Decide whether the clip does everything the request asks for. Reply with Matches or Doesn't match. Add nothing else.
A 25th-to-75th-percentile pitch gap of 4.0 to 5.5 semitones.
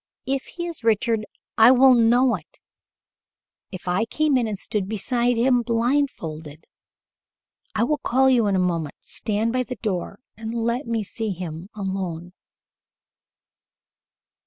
Matches